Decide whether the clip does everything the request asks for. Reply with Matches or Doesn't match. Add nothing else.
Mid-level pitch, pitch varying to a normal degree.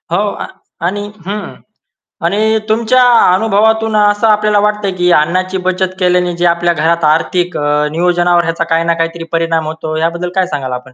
Matches